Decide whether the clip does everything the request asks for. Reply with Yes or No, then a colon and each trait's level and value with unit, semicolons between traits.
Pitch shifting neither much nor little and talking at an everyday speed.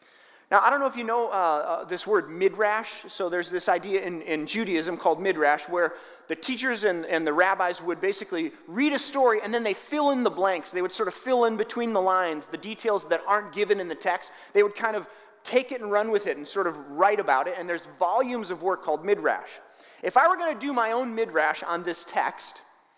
No: average, 4.4 semitones; fast, 240 wpm